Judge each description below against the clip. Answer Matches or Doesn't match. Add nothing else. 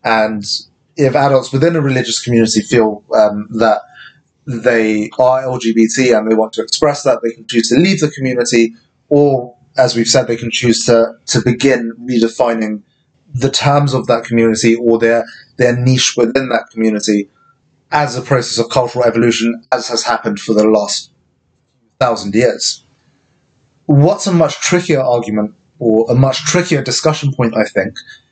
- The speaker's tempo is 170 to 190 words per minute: Doesn't match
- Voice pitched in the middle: Doesn't match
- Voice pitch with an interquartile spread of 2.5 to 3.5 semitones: Matches